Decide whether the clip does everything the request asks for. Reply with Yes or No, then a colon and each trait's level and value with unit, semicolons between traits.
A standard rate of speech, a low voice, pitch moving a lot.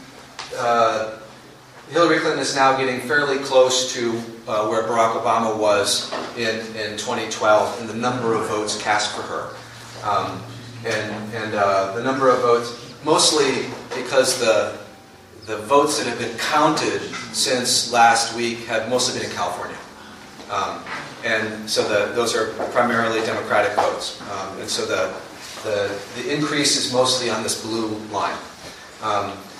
No: average, 150 wpm; low, 115 Hz; narrow, 2.5 semitones